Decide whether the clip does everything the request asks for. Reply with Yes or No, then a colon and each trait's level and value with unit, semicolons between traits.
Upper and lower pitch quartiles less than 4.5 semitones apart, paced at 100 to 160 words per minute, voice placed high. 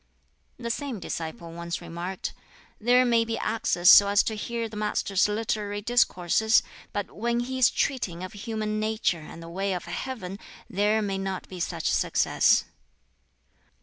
Yes: average, 3.7 semitones; average, 155 wpm; high, 210 Hz